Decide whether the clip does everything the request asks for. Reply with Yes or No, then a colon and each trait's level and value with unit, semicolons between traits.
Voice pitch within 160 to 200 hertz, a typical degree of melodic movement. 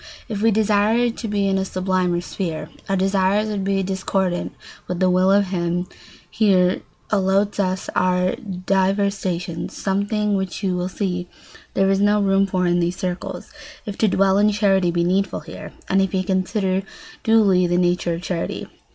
No: high, 190 Hz; narrow, 1.8 semitones